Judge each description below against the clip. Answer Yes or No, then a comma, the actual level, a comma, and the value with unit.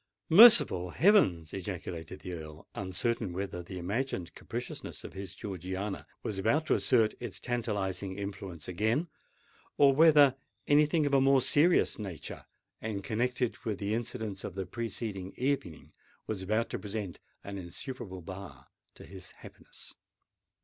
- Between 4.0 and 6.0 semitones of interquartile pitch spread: Yes, average, 5.2 semitones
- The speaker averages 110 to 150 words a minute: Yes, average, 145 wpm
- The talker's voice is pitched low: Yes, low, 100 Hz